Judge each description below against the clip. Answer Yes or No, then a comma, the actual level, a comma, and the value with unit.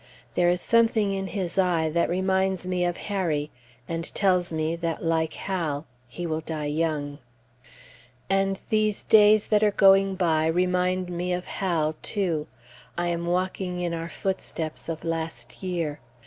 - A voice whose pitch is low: No, medium, 175 Hz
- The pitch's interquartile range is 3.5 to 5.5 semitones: No, average, 2.8 semitones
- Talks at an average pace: Yes, average, 155 wpm